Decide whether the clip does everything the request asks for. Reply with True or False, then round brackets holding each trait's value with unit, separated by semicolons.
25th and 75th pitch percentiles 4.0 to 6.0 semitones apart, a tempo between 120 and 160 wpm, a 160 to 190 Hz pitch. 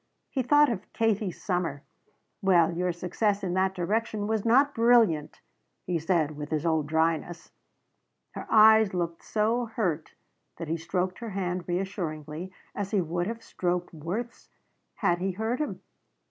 True (4.6 semitones; 150 wpm; 185 Hz)